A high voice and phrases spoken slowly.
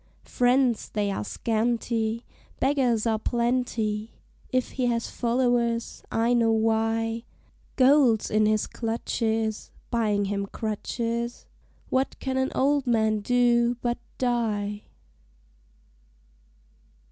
Yes: high, 230 Hz; slow, 100 wpm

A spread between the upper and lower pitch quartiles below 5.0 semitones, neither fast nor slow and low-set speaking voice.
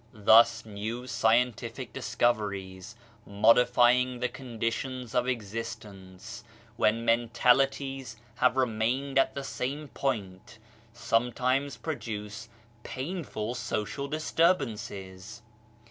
No: average, 2.9 semitones; slow, 85 wpm; low, 120 Hz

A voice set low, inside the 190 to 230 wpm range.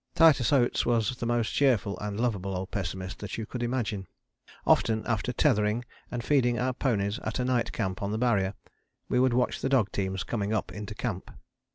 Yes: low, 115 Hz; average, 195 wpm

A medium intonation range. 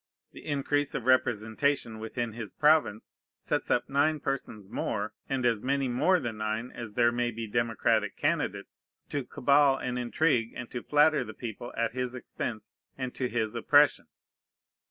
Yes: average, 3.6 semitones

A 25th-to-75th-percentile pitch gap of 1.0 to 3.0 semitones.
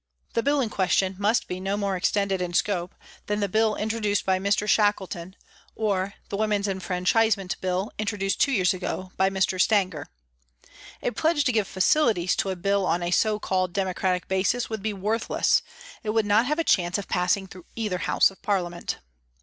Yes: narrow, 2.5 semitones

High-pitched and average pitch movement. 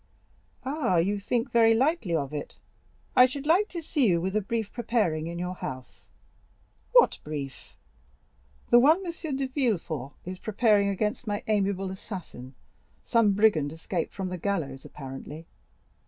No: high, 200 Hz; wide, 6.4 semitones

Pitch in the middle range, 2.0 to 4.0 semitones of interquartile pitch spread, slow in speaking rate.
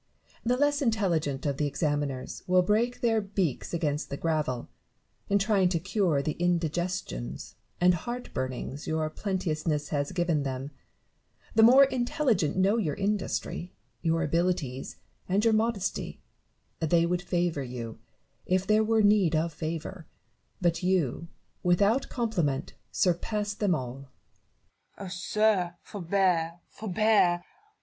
No: medium, 175 Hz; average, 5.0 semitones; slow, 130 wpm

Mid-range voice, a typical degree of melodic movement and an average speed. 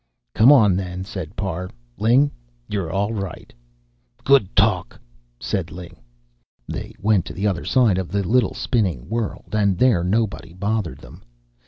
No: low, 100 Hz; average, 3.5 semitones; average, 150 wpm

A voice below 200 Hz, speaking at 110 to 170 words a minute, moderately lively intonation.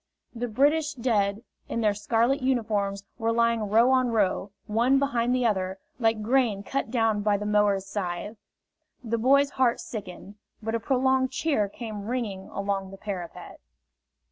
No: high, 225 Hz; average, 155 wpm; average, 3.7 semitones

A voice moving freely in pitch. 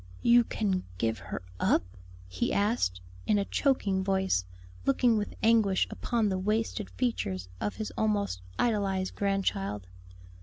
Yes: wide, 8.2 semitones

